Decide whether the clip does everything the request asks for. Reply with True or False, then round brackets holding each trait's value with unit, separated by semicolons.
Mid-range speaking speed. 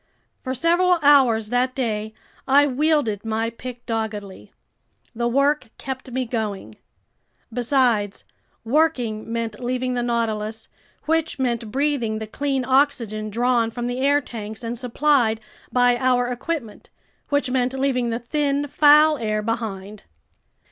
False (130 wpm)